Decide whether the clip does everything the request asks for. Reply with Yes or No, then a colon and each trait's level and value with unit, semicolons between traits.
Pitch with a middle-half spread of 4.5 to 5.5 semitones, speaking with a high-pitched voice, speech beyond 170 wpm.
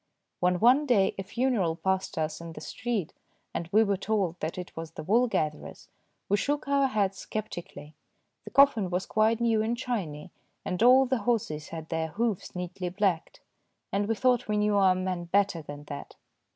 Yes: average, 5.2 semitones; high, 195 Hz; average, 185 wpm